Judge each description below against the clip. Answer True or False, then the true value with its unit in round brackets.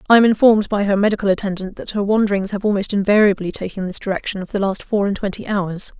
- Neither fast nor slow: False (230 wpm)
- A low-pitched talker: False (200 Hz)